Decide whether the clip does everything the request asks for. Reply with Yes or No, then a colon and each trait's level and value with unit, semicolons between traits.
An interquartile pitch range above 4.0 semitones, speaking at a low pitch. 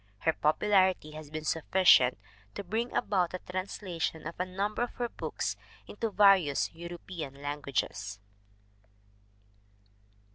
No: average, 4.4 semitones; medium, 175 Hz